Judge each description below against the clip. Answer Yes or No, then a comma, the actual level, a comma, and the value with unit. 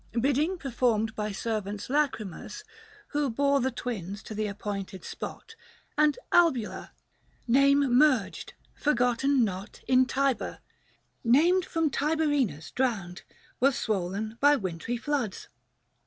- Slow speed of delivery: Yes, slow, 125 wpm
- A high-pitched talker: Yes, high, 245 Hz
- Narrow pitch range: No, average, 5.2 semitones